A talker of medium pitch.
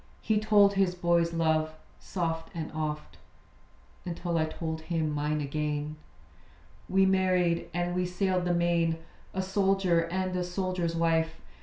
Yes: medium, 170 Hz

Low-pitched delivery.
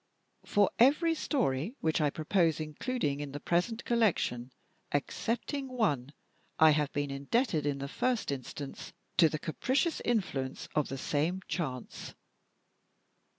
No: medium, 160 Hz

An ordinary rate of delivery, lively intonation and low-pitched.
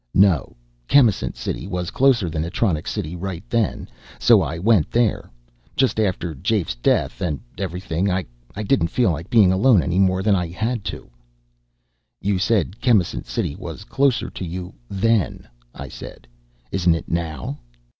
No: average, 155 wpm; average, 4.7 semitones; very low, 95 Hz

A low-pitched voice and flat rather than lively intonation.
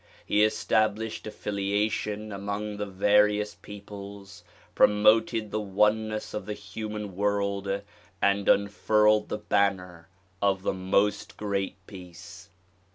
Yes: low, 100 Hz; narrow, 1.2 semitones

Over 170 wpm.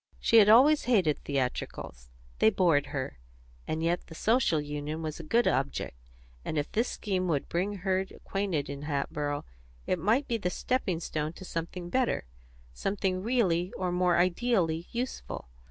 No: average, 160 wpm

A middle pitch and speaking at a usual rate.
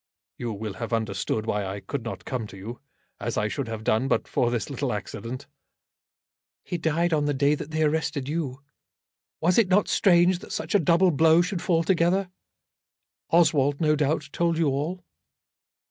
Yes: medium, 150 Hz; average, 180 wpm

